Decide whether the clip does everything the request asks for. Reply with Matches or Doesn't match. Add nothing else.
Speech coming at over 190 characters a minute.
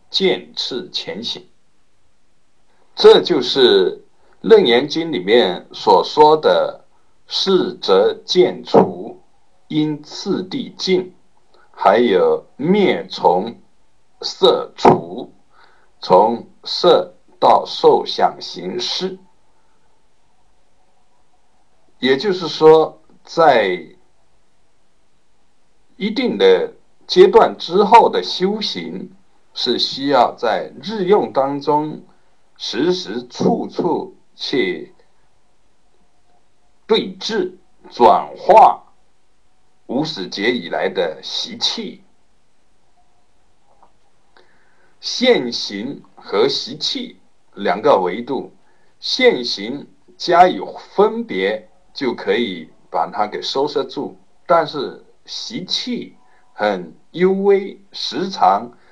Doesn't match